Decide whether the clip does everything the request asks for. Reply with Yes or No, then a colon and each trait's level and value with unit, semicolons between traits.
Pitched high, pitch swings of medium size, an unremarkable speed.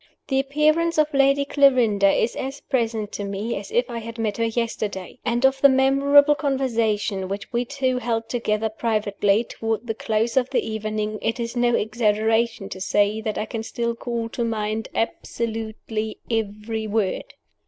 Yes: high, 230 Hz; average, 3.2 semitones; average, 170 wpm